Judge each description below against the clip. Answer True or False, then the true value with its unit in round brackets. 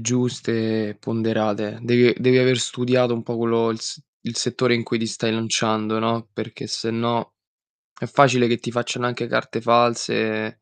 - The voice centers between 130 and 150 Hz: False (115 Hz)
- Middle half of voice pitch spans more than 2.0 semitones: False (1.4 semitones)